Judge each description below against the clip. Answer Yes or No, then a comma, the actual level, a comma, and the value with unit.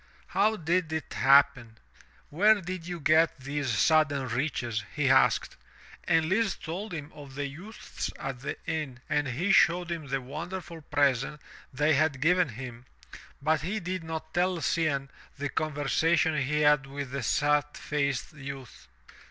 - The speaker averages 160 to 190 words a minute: No, average, 150 wpm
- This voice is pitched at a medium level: Yes, medium, 150 Hz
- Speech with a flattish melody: No, average, 3.4 semitones